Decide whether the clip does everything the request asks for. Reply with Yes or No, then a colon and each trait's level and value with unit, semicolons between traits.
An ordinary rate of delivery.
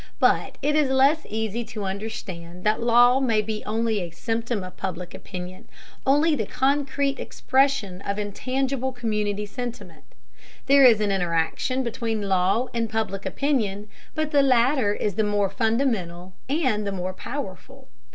Yes: average, 150 wpm